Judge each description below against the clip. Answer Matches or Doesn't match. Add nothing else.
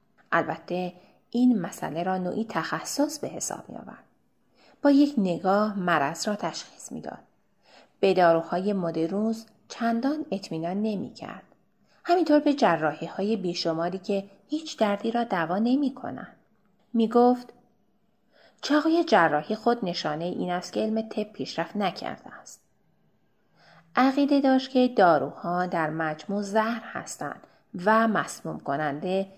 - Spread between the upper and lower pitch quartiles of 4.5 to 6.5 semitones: Matches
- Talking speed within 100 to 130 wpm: Matches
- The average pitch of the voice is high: Matches